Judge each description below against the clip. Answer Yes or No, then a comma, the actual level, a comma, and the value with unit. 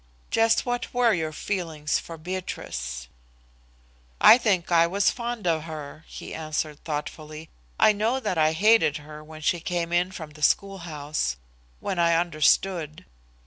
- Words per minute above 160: No, average, 145 wpm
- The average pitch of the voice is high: No, medium, 165 Hz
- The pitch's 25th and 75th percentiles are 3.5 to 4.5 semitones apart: Yes, average, 3.9 semitones